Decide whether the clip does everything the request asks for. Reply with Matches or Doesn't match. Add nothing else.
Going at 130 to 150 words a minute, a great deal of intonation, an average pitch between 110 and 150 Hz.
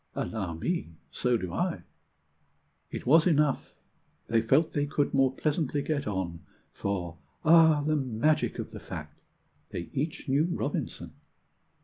Matches